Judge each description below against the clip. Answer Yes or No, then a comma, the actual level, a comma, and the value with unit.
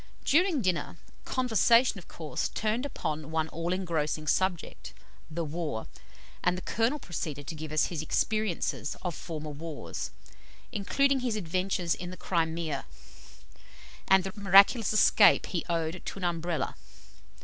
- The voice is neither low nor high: Yes, medium, 175 Hz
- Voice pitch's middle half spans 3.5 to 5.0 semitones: Yes, average, 4.5 semitones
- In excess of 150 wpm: No, average, 140 wpm